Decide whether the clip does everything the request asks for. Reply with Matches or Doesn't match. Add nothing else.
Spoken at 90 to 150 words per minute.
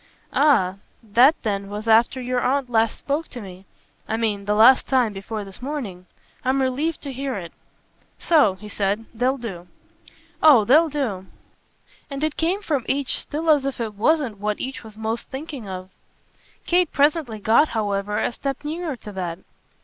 Doesn't match